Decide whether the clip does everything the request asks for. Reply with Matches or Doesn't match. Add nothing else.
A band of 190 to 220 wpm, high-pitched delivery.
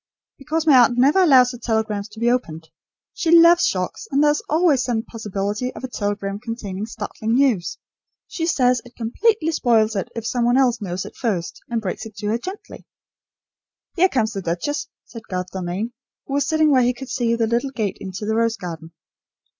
Matches